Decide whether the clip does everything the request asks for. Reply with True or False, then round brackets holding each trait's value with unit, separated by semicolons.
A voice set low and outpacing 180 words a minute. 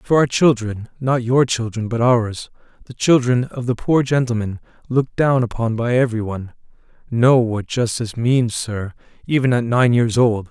False (120 Hz; 155 wpm)